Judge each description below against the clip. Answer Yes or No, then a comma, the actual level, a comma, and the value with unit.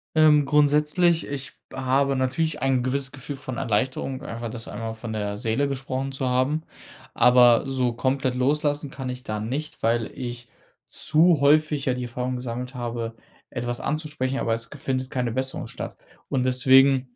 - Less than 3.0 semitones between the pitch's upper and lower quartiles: Yes, narrow, 2.5 semitones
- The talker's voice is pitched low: Yes, low, 130 Hz